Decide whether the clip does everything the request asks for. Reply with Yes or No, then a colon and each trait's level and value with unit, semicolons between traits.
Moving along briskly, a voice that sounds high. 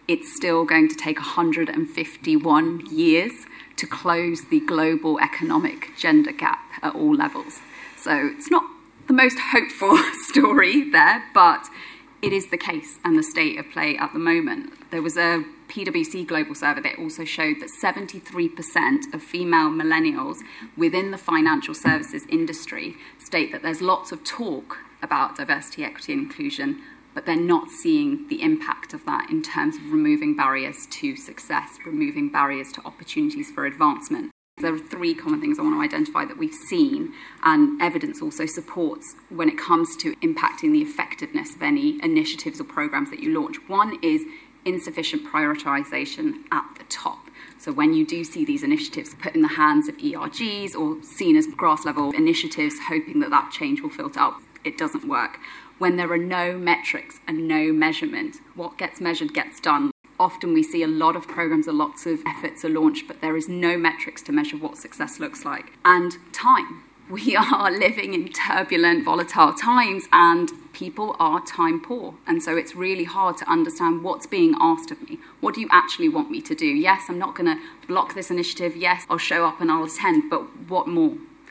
No: average, 180 wpm; very high, 295 Hz